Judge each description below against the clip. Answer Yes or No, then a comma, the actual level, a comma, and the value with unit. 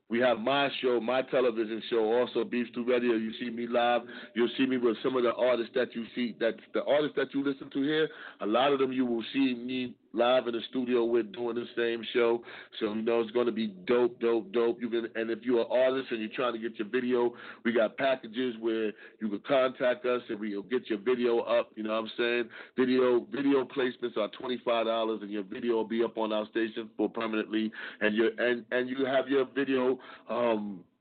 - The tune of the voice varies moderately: No, narrow, 1.9 semitones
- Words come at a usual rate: No, fast, 235 wpm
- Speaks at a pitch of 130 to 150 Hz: No, low, 120 Hz